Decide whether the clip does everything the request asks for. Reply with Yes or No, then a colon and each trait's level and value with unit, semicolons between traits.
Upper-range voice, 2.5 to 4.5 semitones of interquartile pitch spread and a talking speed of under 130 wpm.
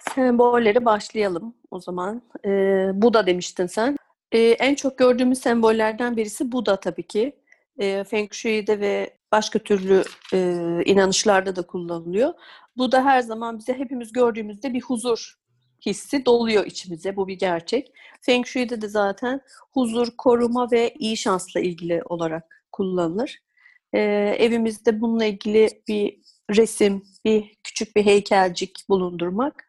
No: high, 220 Hz; average, 4.0 semitones; average, 135 wpm